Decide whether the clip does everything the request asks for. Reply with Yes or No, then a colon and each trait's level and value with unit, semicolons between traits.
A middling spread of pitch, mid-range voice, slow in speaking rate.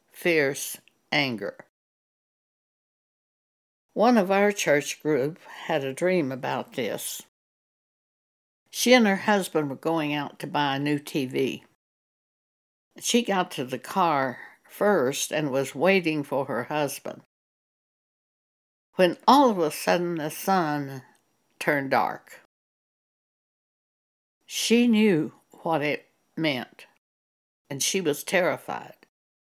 Yes: average, 5.0 semitones; medium, 155 Hz; slow, 110 wpm